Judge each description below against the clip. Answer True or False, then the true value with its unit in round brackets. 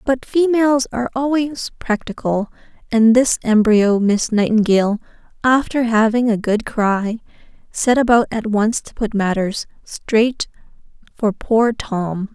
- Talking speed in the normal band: False (125 wpm)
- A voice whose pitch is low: False (225 Hz)